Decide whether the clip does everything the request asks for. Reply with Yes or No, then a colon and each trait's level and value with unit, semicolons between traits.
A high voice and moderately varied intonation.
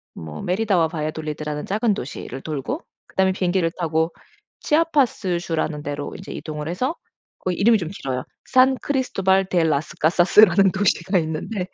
No: medium, 175 Hz; average, 4.4 semitones